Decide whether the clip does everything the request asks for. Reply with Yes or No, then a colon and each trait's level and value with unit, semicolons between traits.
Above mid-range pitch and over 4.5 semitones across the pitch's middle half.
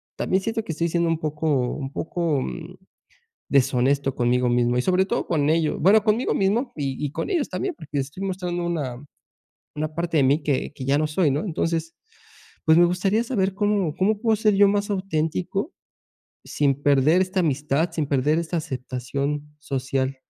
No: medium, 160 Hz; average, 5.2 semitones